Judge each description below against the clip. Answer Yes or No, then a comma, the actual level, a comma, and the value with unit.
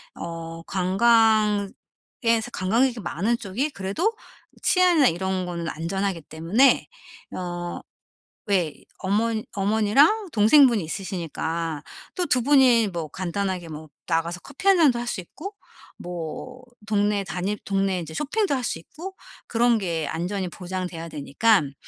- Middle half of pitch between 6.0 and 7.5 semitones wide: No, wide, 5.5 semitones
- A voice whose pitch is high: Yes, high, 195 Hz